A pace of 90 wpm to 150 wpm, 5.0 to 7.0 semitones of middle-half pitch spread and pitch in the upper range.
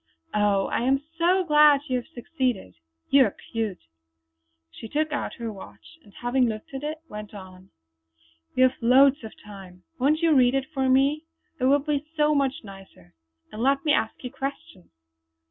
No: average, 180 wpm; average, 5.3 semitones; very high, 260 Hz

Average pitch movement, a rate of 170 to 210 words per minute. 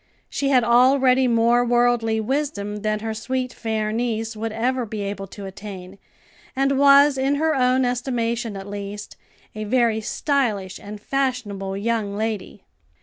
No: average, 3.5 semitones; average, 145 wpm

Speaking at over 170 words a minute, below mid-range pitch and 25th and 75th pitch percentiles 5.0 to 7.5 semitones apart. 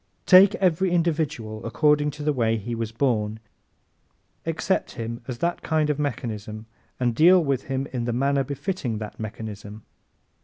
No: average, 155 wpm; low, 130 Hz; wide, 5.5 semitones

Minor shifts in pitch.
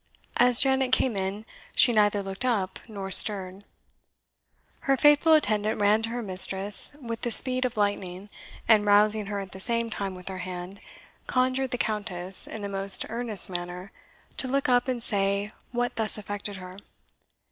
No: average, 3.8 semitones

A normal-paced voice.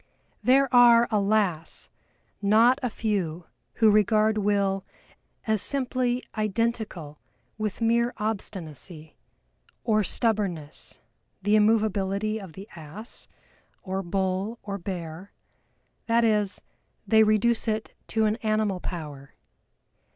No: slow, 105 wpm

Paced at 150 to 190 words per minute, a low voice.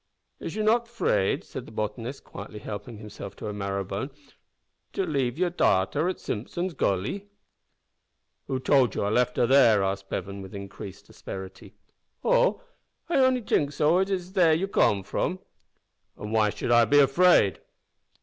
Yes: average, 160 wpm; low, 120 Hz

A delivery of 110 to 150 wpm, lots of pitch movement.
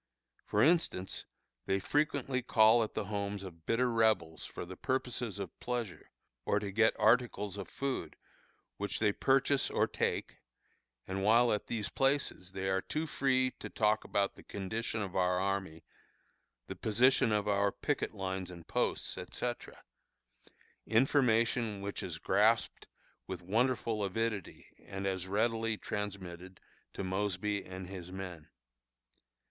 No: average, 140 wpm; average, 3.5 semitones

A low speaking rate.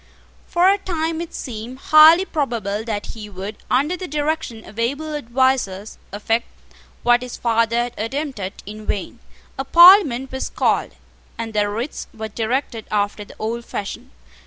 No: average, 155 wpm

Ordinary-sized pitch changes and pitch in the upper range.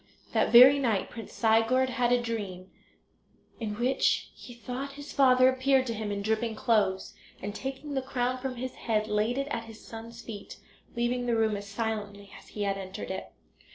Yes: average, 3.3 semitones; high, 230 Hz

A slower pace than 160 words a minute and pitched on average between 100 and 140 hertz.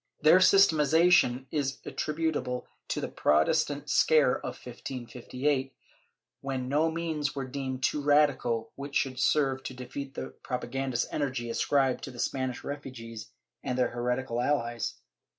Yes: average, 140 wpm; low, 135 Hz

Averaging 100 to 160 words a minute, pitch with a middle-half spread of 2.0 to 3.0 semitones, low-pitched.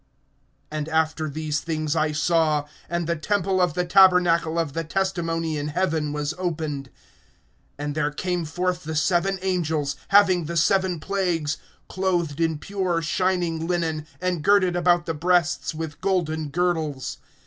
No: average, 150 wpm; narrow, 2.6 semitones; medium, 165 Hz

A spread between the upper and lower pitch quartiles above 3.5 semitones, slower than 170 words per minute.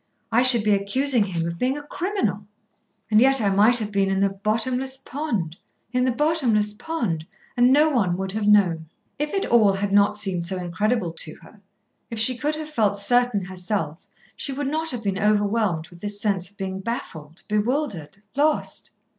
No: average, 4.7 semitones; average, 190 wpm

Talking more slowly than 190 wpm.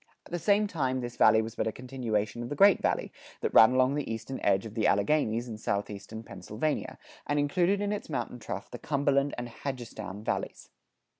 No: average, 200 wpm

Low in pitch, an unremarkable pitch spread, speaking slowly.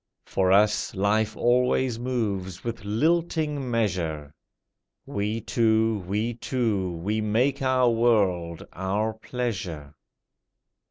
Yes: low, 110 Hz; average, 3.9 semitones; slow, 100 wpm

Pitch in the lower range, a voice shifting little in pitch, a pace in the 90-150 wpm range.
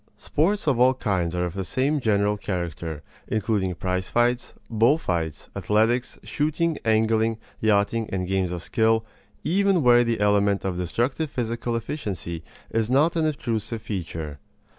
No: low, 110 Hz; average, 4.8 semitones; average, 145 wpm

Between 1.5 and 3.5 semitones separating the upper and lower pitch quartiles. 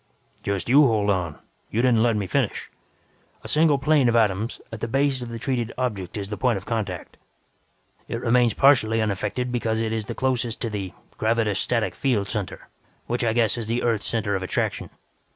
Yes: average, 2.9 semitones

